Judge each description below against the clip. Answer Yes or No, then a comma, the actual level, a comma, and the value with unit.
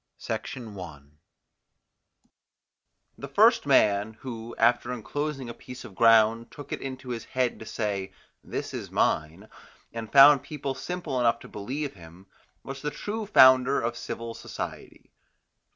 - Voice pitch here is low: Yes, low, 120 Hz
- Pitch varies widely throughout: No, average, 3.7 semitones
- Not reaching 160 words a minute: Yes, average, 140 wpm